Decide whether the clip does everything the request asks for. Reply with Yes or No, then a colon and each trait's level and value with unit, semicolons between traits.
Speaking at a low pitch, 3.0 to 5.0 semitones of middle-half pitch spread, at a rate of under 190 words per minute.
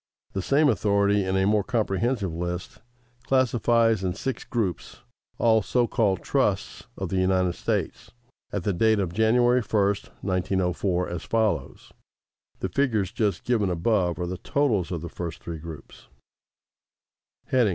Yes: low, 100 Hz; average, 4.1 semitones; average, 145 wpm